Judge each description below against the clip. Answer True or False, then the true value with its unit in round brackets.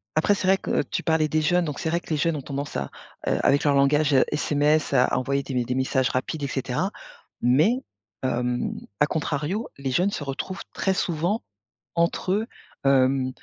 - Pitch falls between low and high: True (145 Hz)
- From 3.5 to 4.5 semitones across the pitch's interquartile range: True (4.1 semitones)